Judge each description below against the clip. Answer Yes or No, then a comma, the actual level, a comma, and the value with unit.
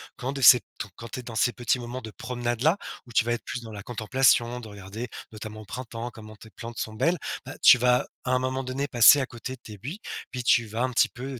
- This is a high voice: No, low, 120 Hz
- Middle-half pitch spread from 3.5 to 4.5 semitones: No, narrow, 2.4 semitones